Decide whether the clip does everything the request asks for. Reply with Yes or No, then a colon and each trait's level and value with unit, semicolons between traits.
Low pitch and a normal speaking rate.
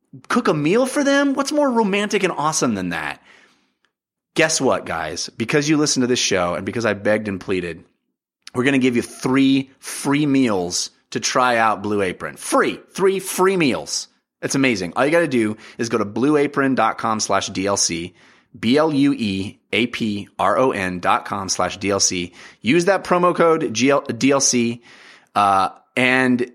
Yes: low, 125 Hz; average, 150 wpm